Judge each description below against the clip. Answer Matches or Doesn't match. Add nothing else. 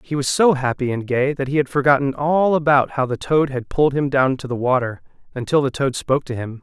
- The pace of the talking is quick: Matches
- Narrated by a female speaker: Doesn't match